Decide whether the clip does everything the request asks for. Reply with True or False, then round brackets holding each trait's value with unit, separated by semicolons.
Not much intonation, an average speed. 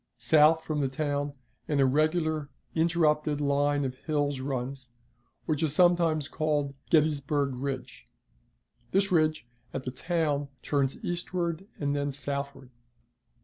False (2.1 semitones; 125 wpm)